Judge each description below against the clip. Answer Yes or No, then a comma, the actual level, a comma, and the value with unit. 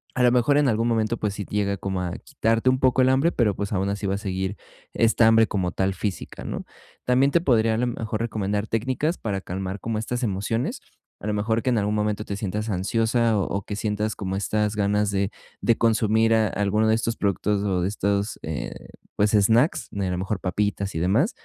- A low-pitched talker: Yes, low, 105 Hz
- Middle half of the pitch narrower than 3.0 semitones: Yes, narrow, 2.4 semitones